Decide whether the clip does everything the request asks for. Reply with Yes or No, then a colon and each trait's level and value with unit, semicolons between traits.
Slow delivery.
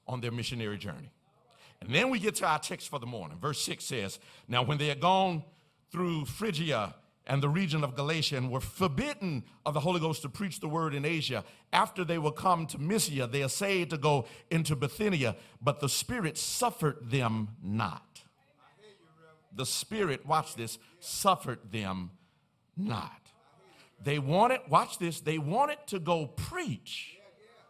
No: average, 165 wpm